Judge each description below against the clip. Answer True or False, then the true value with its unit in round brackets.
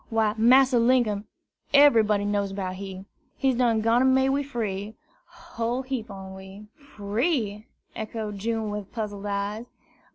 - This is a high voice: True (220 Hz)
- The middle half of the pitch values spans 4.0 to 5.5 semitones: False (3.3 semitones)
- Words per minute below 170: True (135 wpm)